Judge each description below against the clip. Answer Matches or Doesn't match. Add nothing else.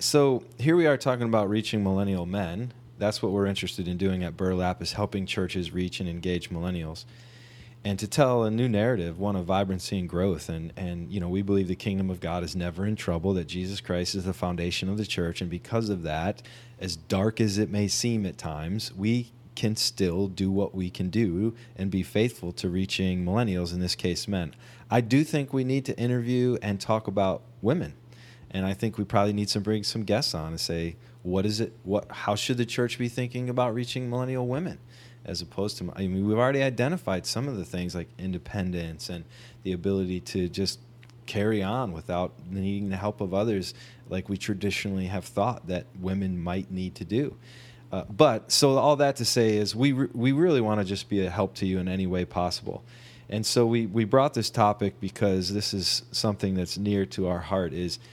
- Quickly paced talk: Matches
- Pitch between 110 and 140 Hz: Doesn't match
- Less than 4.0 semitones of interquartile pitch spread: Doesn't match